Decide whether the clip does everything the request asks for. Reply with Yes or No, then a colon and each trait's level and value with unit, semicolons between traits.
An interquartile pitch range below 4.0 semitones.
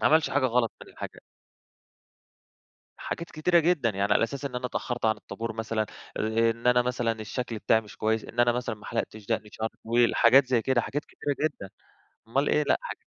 Yes: average, 3.2 semitones